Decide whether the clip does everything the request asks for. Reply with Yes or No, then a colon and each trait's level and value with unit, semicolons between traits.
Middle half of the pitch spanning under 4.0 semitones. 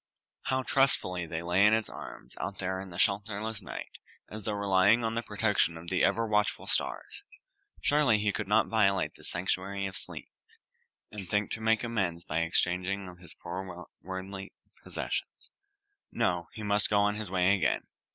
Yes: average, 2.8 semitones